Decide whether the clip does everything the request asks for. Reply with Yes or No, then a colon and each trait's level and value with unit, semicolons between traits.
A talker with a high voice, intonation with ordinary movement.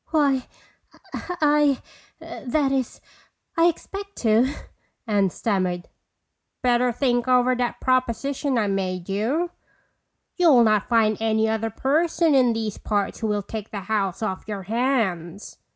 Yes: high, 235 Hz; average, 4.5 semitones